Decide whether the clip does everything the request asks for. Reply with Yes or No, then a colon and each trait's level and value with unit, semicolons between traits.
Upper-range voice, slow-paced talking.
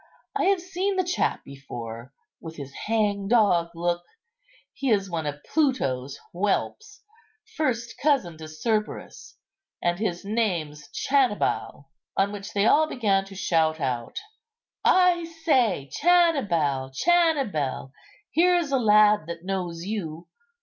Yes: high, 200 Hz; slow, 120 wpm